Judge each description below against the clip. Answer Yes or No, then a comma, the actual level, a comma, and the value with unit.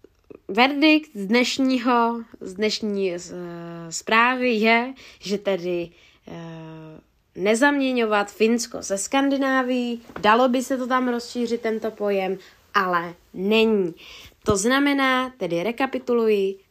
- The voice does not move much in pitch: No, average, 4.6 semitones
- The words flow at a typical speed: No, slow, 110 wpm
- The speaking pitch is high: Yes, high, 225 Hz